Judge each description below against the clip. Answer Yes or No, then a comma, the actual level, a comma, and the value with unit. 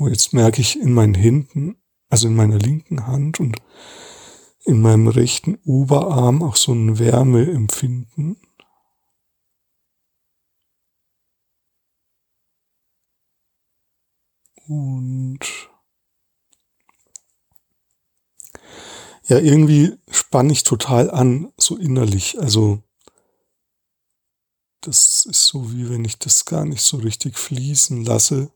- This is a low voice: Yes, low, 130 Hz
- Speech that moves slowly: Yes, slow, 90 wpm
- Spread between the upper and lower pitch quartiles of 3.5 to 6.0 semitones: Yes, average, 4.2 semitones